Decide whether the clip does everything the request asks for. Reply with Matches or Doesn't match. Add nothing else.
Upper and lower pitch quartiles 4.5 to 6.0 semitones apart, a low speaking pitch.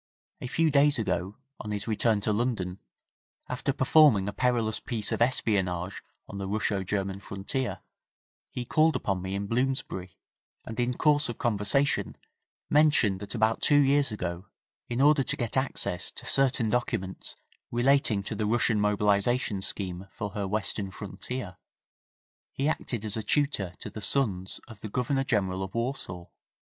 Matches